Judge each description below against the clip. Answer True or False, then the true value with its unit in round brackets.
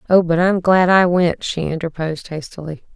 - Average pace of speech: True (185 wpm)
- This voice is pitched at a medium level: True (170 Hz)